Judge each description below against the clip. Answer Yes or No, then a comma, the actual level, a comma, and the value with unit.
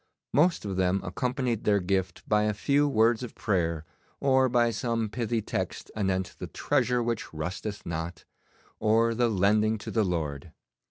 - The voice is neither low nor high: No, low, 105 Hz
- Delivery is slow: No, average, 160 wpm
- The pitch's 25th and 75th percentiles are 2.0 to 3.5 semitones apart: No, average, 4.1 semitones